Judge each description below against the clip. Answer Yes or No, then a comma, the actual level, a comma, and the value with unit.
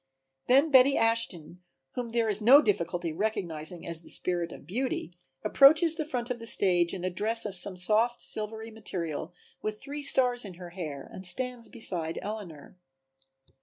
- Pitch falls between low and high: No, high, 210 Hz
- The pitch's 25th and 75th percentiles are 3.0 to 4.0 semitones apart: No, wide, 5.6 semitones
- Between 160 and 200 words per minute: Yes, average, 170 wpm